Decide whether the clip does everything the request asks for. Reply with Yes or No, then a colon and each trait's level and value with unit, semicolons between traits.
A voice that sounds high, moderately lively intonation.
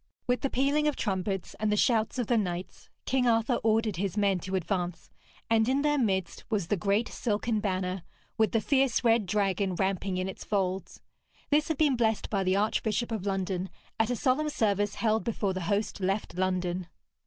Yes: high, 210 Hz; average, 3.6 semitones